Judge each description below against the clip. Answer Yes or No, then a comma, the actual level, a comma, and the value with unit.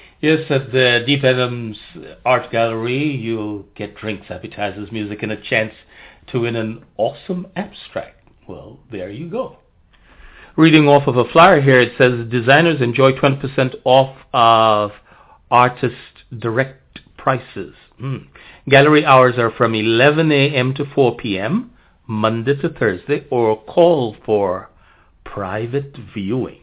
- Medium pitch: No, low, 125 Hz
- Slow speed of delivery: Yes, slow, 130 wpm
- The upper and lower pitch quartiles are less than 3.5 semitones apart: No, average, 3.9 semitones